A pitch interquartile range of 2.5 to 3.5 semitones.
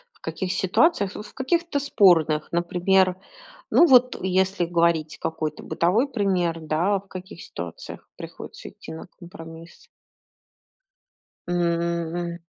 Yes: average, 2.9 semitones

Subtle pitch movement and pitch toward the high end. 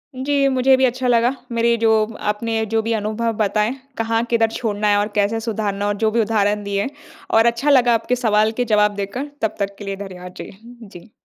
Yes: narrow, 2.3 semitones; high, 225 Hz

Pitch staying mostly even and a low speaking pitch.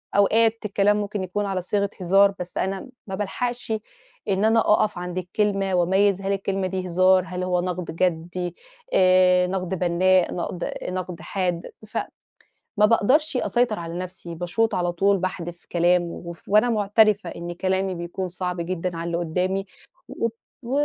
No: narrow, 2.3 semitones; medium, 185 Hz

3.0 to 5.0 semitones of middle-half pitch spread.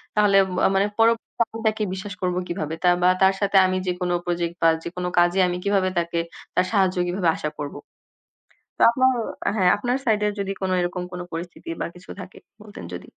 No: narrow, 2.5 semitones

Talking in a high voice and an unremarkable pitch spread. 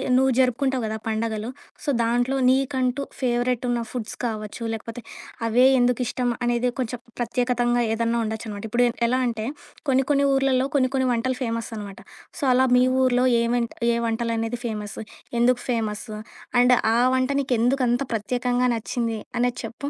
No: high, 245 Hz; narrow, 1.9 semitones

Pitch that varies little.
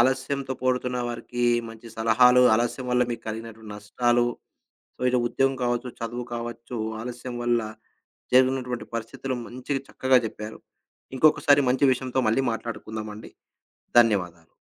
Yes: narrow, 2.2 semitones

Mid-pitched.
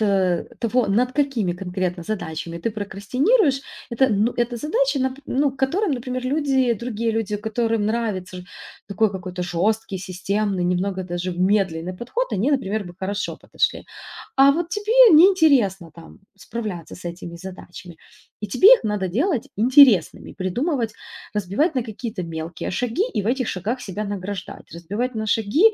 No: high, 215 Hz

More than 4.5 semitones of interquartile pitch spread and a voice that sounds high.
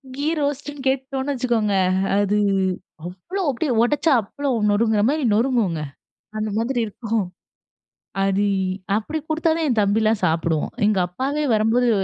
Yes: average, 5.2 semitones; high, 230 Hz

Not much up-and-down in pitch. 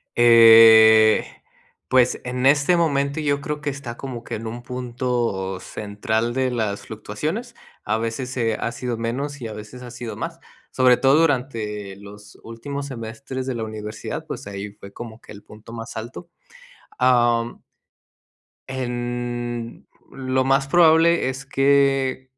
No: average, 3.2 semitones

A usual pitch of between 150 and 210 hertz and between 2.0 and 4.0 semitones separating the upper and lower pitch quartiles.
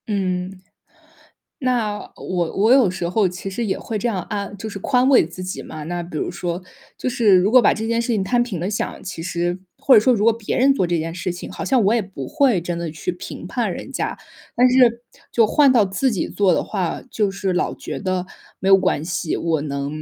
No: high, 195 Hz; average, 4.8 semitones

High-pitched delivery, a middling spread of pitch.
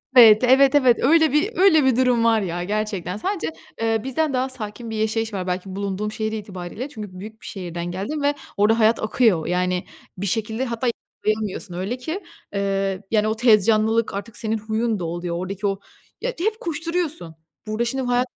Yes: high, 220 Hz; average, 4.5 semitones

